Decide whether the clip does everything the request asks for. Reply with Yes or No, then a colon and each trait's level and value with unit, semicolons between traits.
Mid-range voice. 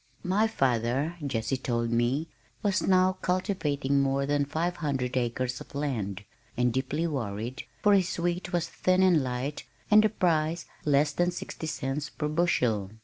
Yes: medium, 145 Hz